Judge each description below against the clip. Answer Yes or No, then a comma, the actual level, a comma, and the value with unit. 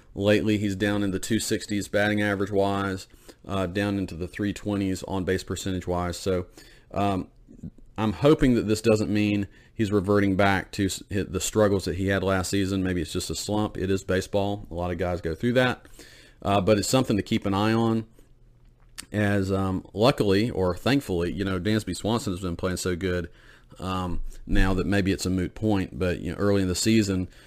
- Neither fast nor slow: Yes, average, 190 wpm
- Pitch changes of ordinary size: No, narrow, 2.2 semitones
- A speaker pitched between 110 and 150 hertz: No, low, 100 Hz